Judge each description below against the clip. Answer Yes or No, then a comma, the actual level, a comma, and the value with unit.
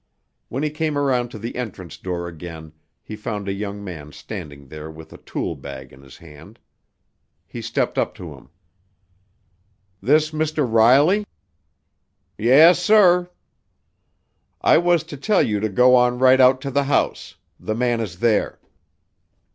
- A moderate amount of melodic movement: No, wide, 8.6 semitones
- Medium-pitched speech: No, low, 115 Hz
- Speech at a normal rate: Yes, average, 155 wpm